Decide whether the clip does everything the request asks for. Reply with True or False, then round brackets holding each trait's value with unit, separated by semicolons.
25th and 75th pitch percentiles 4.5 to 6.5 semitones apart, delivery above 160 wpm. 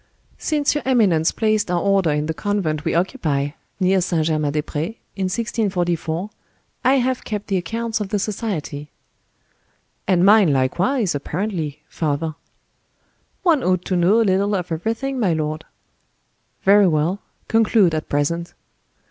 False (5.2 semitones; 145 wpm)